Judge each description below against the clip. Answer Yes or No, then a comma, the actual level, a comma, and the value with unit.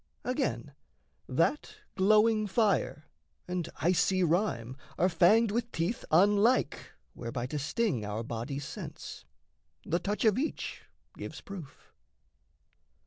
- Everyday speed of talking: No, slow, 110 wpm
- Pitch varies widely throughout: Yes, wide, 7.0 semitones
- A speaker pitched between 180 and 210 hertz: Yes, medium, 185 Hz